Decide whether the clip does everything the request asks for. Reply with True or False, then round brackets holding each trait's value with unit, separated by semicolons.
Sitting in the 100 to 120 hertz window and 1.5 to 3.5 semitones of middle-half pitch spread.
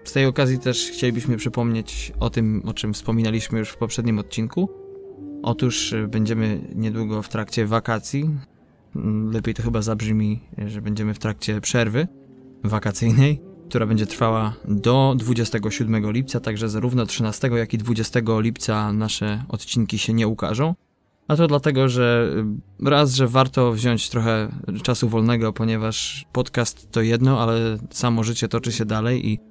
True (115 Hz; 2.6 semitones)